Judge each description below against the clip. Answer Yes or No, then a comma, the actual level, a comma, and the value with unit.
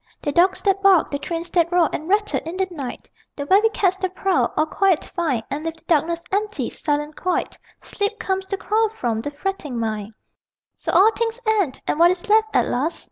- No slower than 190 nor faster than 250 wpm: Yes, fast, 205 wpm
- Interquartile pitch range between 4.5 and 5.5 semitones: Yes, average, 4.8 semitones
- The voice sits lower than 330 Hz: No, very high, 350 Hz